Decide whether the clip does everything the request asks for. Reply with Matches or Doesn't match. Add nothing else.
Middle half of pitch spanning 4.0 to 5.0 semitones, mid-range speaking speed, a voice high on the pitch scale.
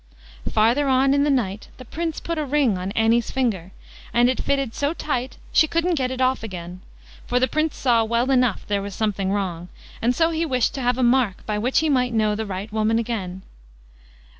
Doesn't match